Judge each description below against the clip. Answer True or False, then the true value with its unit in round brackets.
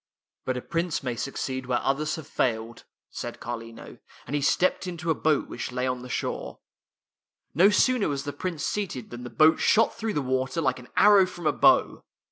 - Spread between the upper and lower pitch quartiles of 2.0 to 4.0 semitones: False (5.1 semitones)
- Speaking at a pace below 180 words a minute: False (205 wpm)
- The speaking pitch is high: False (140 Hz)